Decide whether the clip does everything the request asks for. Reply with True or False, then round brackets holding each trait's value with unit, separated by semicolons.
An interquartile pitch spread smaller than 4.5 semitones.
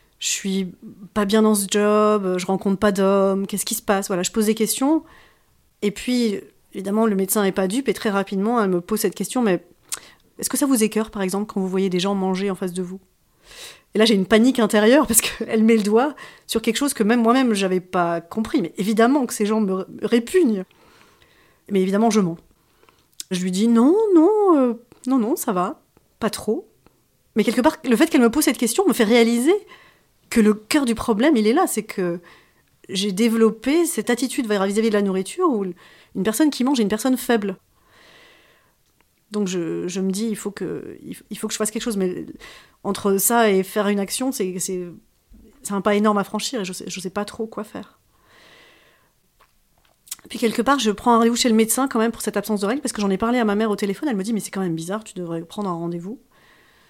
True (3.3 semitones)